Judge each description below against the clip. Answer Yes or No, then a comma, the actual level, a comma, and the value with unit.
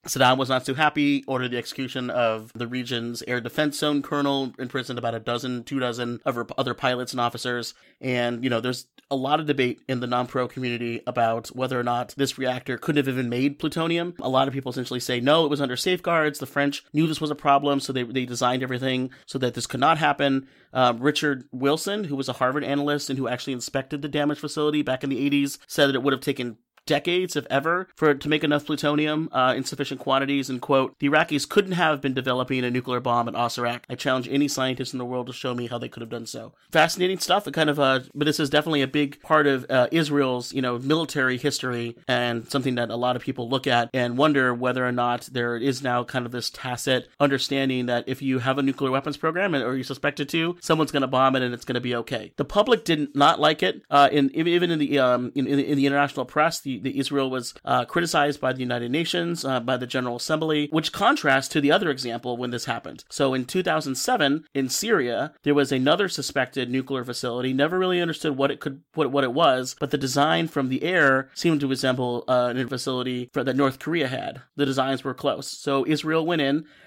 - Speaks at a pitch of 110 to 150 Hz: Yes, low, 135 Hz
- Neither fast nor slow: No, fast, 235 wpm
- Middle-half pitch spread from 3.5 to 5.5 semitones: No, narrow, 2.6 semitones